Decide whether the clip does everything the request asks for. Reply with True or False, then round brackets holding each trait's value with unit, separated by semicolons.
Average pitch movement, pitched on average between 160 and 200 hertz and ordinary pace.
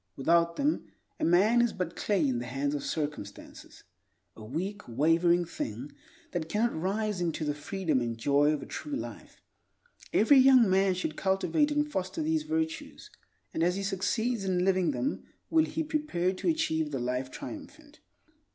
False (7.9 semitones; 185 Hz; 170 wpm)